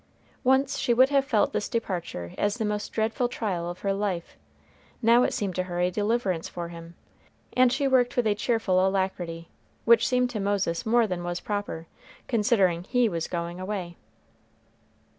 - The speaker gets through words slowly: No, average, 175 wpm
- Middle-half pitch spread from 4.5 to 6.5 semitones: Yes, average, 5.0 semitones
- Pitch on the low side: No, high, 205 Hz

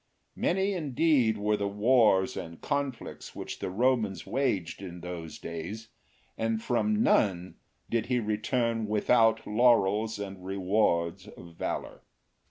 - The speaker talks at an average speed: No, slow, 125 wpm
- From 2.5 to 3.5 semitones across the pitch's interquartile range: No, average, 4.3 semitones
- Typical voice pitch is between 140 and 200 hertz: No, low, 110 Hz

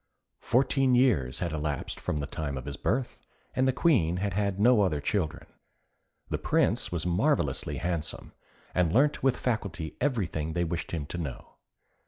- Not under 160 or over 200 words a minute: Yes, average, 165 wpm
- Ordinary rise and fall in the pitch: No, wide, 7.8 semitones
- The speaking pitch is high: No, very low, 90 Hz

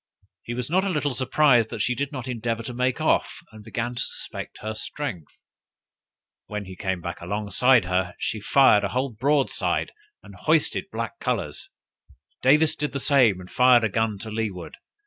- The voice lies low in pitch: Yes, low, 120 Hz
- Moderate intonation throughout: Yes, average, 4.1 semitones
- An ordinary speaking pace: Yes, average, 180 wpm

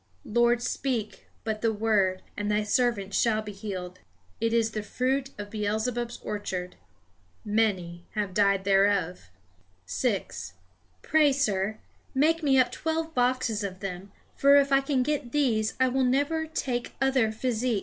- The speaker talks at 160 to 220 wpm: No, average, 150 wpm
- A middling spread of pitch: Yes, average, 4.3 semitones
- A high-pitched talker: Yes, high, 225 Hz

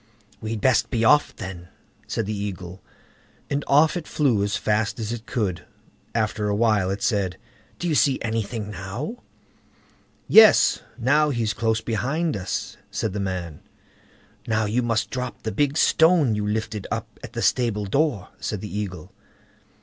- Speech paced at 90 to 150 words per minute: No, average, 160 wpm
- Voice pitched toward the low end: Yes, low, 110 Hz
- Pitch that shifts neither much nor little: Yes, average, 3.8 semitones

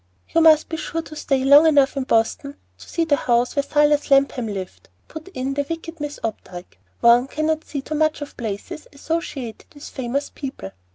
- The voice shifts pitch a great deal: No, average, 3.8 semitones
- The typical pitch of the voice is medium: No, very high, 285 Hz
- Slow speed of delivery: No, average, 190 wpm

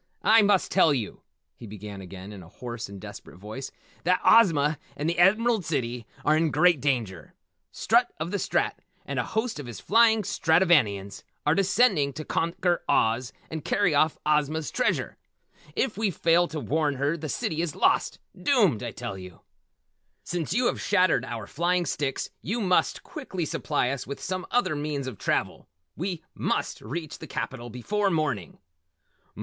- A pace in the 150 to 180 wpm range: Yes, average, 170 wpm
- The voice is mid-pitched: Yes, medium, 155 Hz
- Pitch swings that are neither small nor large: No, wide, 6.6 semitones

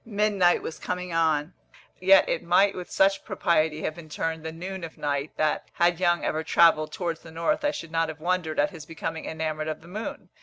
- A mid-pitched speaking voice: Yes, medium, 165 Hz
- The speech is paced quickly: Yes, fast, 215 wpm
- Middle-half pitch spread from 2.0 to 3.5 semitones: Yes, narrow, 2.4 semitones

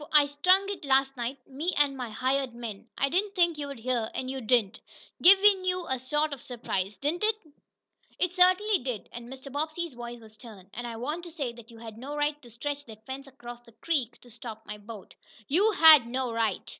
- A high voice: Yes, very high, 265 Hz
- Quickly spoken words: Yes, fast, 215 wpm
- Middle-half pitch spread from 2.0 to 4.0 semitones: No, average, 4.5 semitones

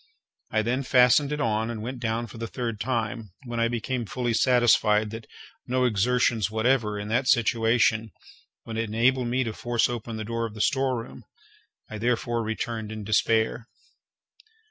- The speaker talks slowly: No, average, 165 wpm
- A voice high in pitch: No, low, 115 Hz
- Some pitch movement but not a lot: No, narrow, 2.0 semitones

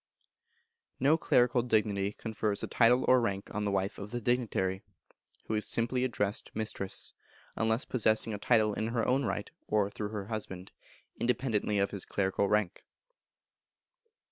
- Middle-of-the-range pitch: No, low, 110 Hz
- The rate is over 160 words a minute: No, average, 150 wpm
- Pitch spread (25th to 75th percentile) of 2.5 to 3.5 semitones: Yes, average, 2.9 semitones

